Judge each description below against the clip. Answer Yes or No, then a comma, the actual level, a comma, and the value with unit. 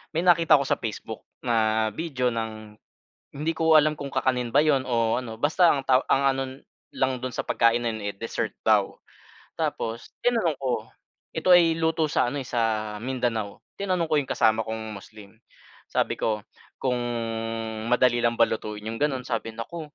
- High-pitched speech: No, low, 125 Hz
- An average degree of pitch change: Yes, average, 4.7 semitones